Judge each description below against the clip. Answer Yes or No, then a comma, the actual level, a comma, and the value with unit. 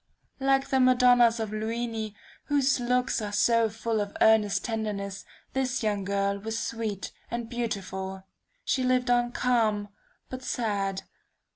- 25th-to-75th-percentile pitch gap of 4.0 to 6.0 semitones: No, average, 3.2 semitones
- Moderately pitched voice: No, high, 225 Hz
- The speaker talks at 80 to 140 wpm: Yes, slow, 135 wpm